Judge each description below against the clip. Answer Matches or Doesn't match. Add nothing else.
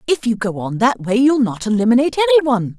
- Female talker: Matches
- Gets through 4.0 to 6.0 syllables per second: Doesn't match